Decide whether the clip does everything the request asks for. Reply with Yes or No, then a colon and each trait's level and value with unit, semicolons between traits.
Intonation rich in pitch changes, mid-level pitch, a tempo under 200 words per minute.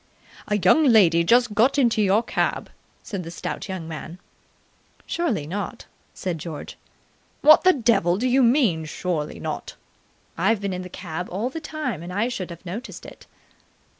No: wide, 5.8 semitones; high, 200 Hz; average, 165 wpm